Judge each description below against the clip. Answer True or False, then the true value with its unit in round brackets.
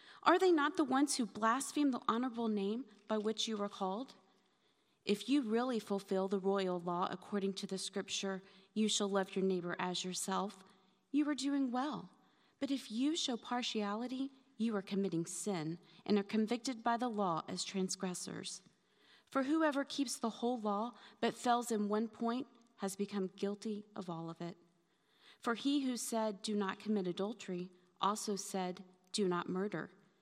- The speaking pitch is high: True (205 Hz)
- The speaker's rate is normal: True (170 wpm)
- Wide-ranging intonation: False (3.9 semitones)